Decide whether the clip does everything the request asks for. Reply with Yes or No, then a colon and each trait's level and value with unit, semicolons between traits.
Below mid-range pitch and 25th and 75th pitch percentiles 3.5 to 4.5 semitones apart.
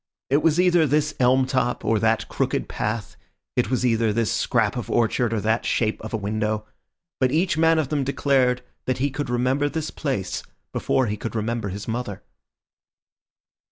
Yes: low, 125 Hz; average, 4.2 semitones